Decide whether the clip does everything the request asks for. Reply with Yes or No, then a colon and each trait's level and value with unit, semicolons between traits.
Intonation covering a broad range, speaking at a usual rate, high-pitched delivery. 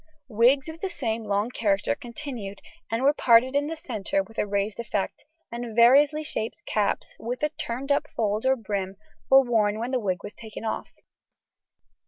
No: average, 4.3 semitones; average, 175 wpm; high, 235 Hz